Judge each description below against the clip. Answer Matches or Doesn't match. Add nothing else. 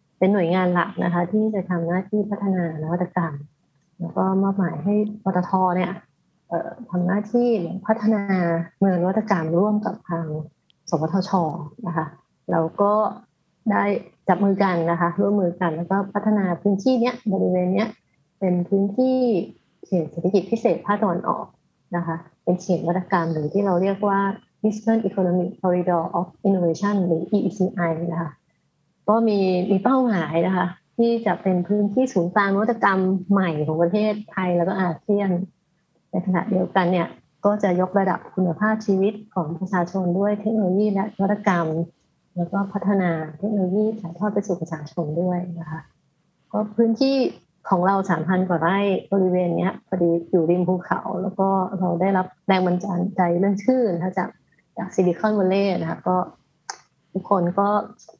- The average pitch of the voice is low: Doesn't match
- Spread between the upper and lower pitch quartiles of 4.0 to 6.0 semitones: Doesn't match